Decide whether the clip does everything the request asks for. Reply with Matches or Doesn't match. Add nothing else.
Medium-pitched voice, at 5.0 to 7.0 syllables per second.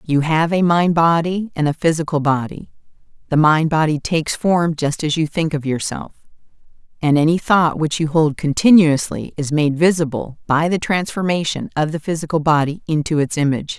Matches